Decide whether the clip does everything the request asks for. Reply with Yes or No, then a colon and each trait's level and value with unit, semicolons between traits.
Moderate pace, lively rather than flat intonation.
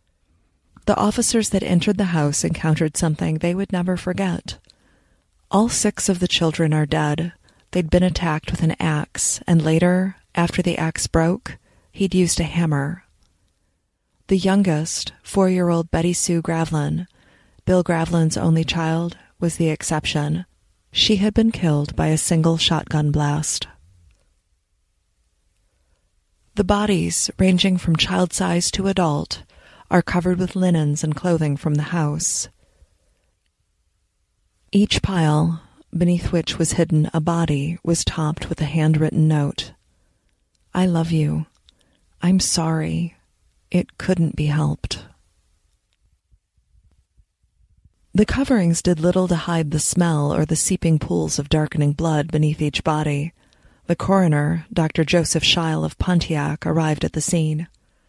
No: slow, 130 wpm; wide, 8.0 semitones